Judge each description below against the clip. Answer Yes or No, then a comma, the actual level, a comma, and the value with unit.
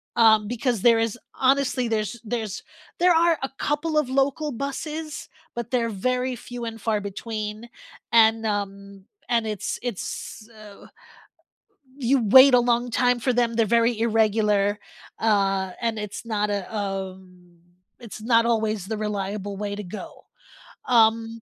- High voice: Yes, high, 225 Hz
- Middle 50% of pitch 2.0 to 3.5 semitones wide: Yes, average, 2.9 semitones